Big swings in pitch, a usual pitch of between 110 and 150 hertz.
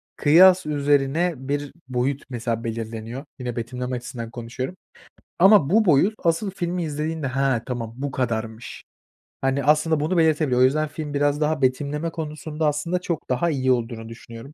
No: average, 4.0 semitones; medium, 140 Hz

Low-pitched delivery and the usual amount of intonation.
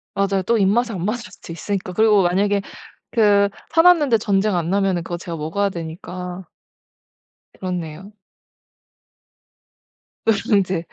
No: high, 195 Hz; average, 3.0 semitones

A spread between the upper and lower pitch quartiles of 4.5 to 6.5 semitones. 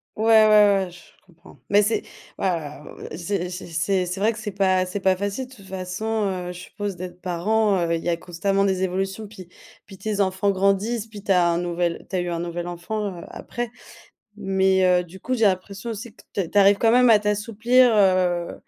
No: average, 2.8 semitones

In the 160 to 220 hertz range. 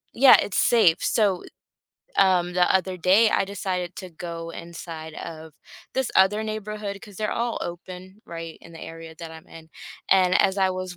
Yes: medium, 185 Hz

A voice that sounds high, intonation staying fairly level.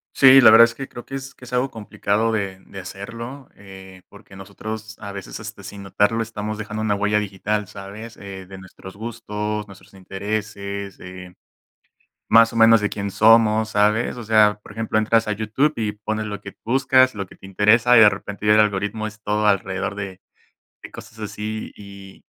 No: low, 105 Hz; narrow, 2.0 semitones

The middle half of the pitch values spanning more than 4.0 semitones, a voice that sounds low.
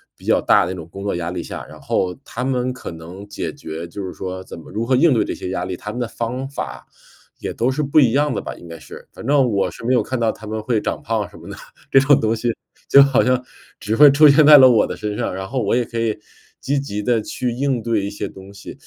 Yes: average, 4.7 semitones; low, 115 Hz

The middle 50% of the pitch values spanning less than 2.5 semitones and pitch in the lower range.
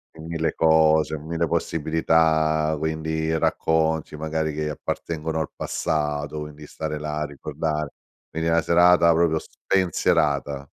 Yes: narrow, 1.1 semitones; very low, 80 Hz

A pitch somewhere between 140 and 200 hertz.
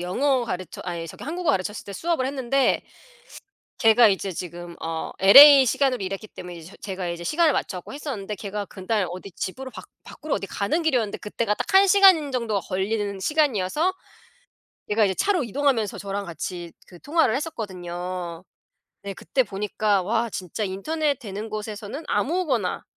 No: high, 210 Hz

